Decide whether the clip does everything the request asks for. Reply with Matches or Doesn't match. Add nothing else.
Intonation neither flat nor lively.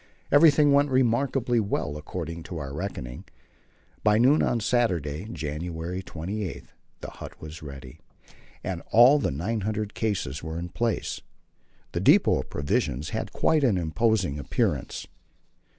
Doesn't match